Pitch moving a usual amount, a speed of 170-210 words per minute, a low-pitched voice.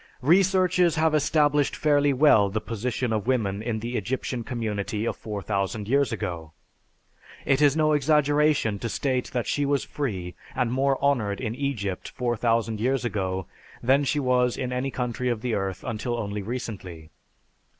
No: average, 4.8 semitones; average, 160 wpm; low, 125 Hz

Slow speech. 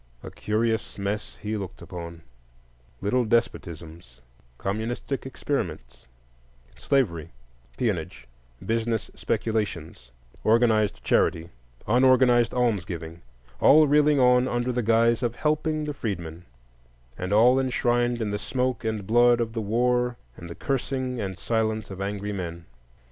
Yes: slow, 120 wpm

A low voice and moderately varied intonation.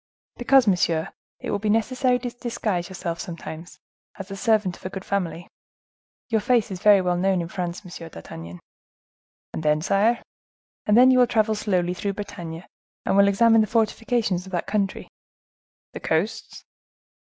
No: high, 195 Hz; average, 4.1 semitones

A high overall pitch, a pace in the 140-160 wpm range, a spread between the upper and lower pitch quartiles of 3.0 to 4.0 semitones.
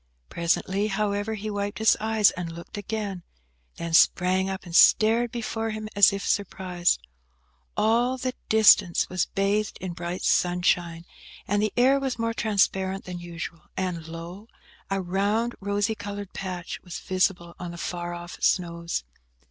Yes: high, 195 Hz; average, 150 wpm; average, 3.4 semitones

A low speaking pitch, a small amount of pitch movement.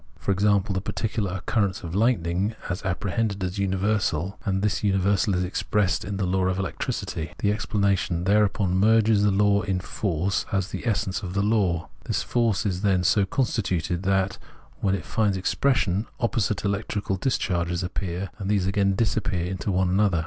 Yes: low, 100 Hz; narrow, 2.0 semitones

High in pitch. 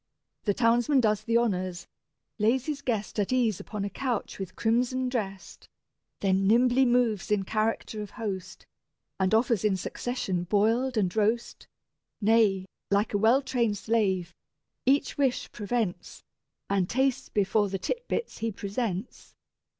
Yes: high, 220 Hz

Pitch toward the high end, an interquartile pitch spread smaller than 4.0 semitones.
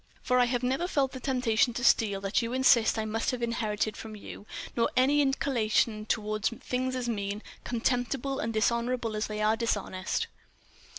Yes: high, 235 Hz; average, 2.8 semitones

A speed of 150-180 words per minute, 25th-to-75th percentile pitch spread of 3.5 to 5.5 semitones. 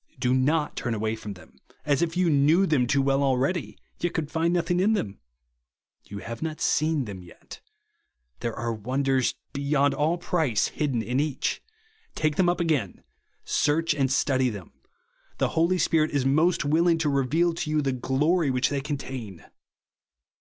Yes: average, 170 wpm; average, 4.1 semitones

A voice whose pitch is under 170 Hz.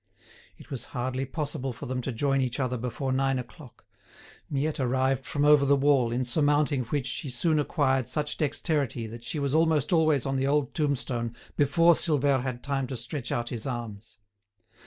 Yes: low, 135 Hz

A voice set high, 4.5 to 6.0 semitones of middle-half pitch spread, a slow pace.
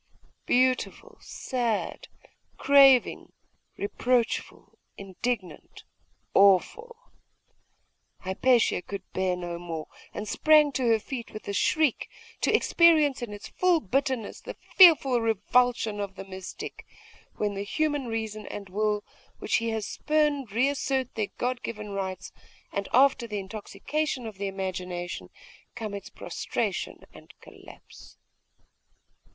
Yes: high, 225 Hz; average, 4.9 semitones; slow, 120 wpm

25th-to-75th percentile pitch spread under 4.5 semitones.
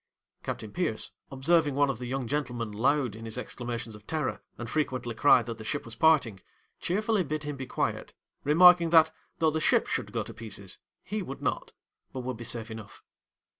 No: average, 5.2 semitones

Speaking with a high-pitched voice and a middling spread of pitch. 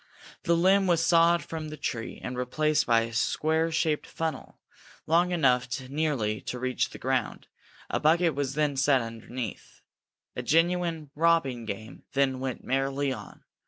No: medium, 145 Hz; average, 4.5 semitones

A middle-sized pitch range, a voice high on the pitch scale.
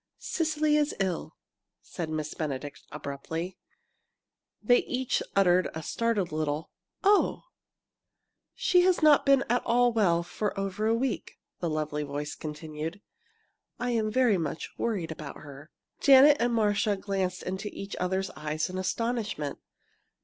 No: wide, 7.2 semitones; high, 195 Hz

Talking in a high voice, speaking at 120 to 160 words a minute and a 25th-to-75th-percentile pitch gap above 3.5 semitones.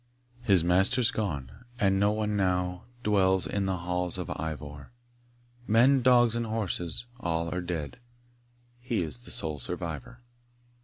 No: very low, 95 Hz; average, 140 wpm; average, 4.6 semitones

